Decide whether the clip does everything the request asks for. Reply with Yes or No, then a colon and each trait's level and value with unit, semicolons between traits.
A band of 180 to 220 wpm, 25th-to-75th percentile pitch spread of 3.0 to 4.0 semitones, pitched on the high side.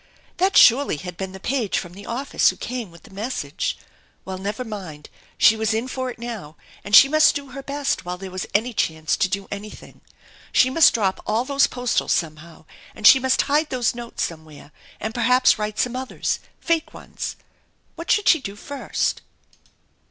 No: average, 190 wpm; wide, 5.4 semitones; high, 225 Hz